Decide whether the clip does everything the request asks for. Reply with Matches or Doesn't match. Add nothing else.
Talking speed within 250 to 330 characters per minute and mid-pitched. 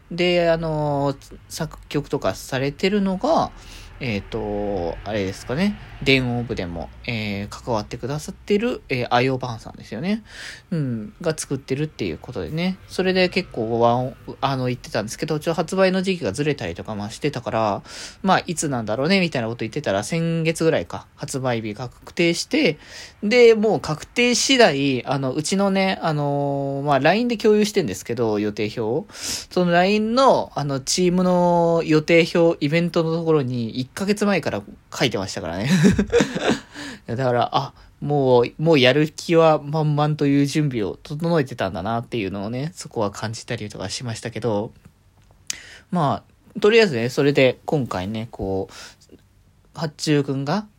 Matches